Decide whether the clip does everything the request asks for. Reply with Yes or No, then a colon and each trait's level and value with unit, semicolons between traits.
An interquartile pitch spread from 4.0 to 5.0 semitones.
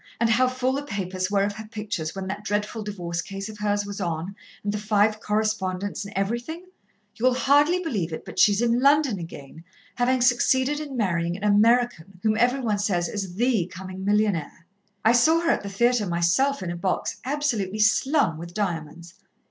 Yes: average, 4.6 semitones